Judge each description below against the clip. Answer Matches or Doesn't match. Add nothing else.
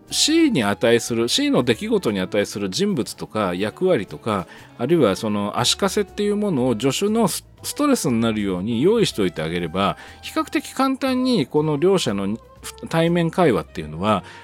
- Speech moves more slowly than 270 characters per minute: Doesn't match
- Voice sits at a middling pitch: Matches